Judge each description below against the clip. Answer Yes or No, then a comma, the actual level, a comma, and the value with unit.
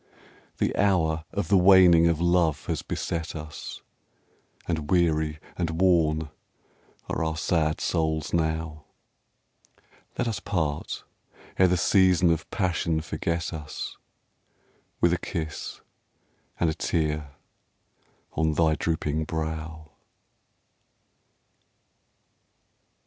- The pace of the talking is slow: Yes, slow, 100 wpm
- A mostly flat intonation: Yes, narrow, 1.8 semitones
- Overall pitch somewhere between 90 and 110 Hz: No, very low, 80 Hz